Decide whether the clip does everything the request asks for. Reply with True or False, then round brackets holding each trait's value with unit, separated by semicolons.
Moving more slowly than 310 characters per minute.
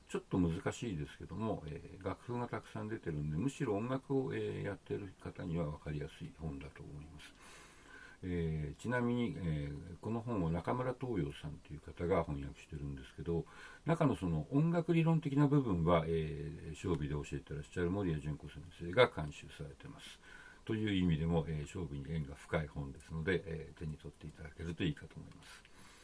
False (390 characters per minute)